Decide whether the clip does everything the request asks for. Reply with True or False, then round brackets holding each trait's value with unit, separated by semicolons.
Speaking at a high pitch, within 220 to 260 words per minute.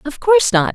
True (295 Hz; 240 wpm)